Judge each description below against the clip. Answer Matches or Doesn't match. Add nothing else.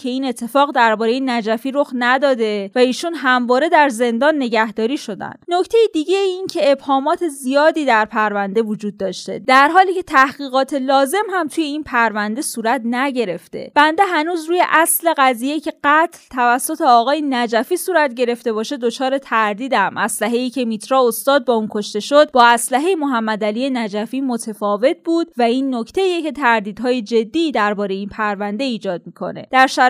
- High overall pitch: Matches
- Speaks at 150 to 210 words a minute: Matches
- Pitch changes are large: Doesn't match